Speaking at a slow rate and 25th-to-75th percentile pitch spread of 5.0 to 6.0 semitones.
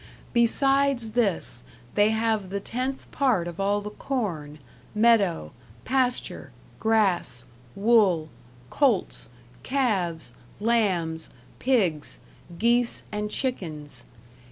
Yes: slow, 90 wpm; wide, 5.6 semitones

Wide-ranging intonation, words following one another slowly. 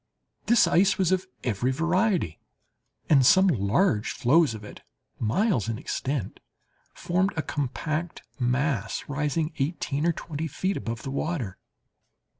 Yes: wide, 6.1 semitones; slow, 125 wpm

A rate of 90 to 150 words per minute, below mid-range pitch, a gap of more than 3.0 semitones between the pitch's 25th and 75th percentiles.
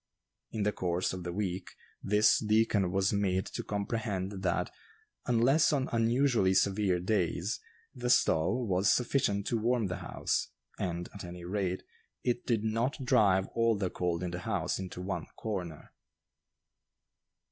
Yes: average, 145 wpm; low, 100 Hz; average, 3.8 semitones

